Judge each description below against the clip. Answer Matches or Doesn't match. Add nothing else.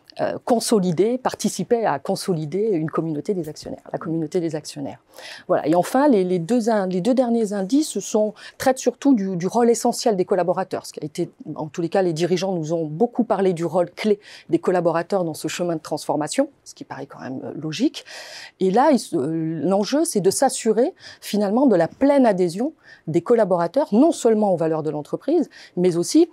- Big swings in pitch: Matches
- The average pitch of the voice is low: Doesn't match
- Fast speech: Doesn't match